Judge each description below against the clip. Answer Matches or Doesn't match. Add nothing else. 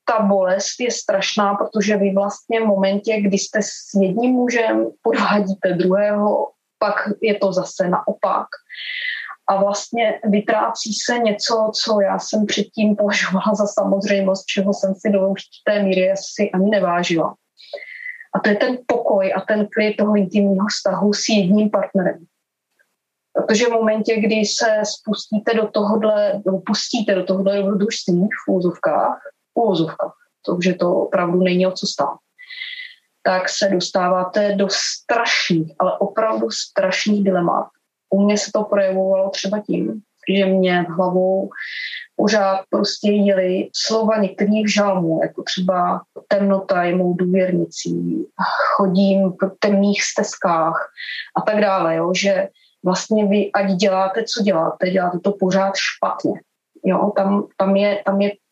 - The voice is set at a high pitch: Matches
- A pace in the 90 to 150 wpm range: Matches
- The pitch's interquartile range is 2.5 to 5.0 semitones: Doesn't match